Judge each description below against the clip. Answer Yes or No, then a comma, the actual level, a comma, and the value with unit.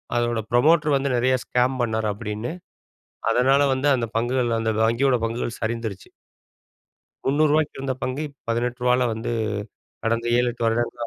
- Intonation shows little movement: Yes, narrow, 2.3 semitones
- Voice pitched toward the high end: No, low, 120 Hz